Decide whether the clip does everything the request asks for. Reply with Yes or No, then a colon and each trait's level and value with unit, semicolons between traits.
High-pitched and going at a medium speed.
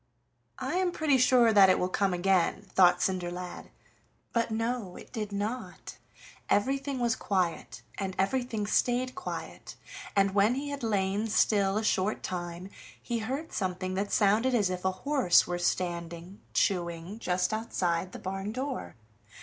Yes: high, 200 Hz; average, 150 wpm